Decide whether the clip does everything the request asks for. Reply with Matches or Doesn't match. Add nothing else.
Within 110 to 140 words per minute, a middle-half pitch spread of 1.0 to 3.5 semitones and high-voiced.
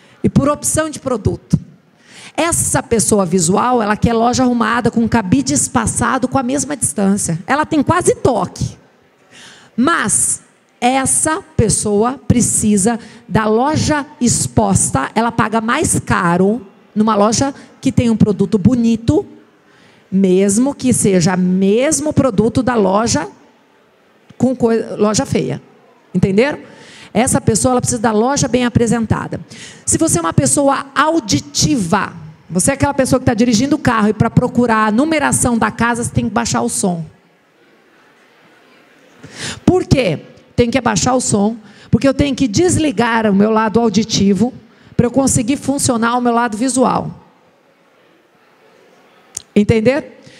Doesn't match